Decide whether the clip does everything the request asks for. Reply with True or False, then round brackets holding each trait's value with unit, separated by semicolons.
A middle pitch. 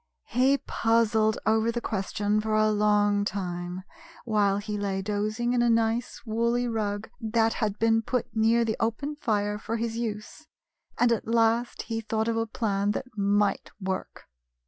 False (220 Hz)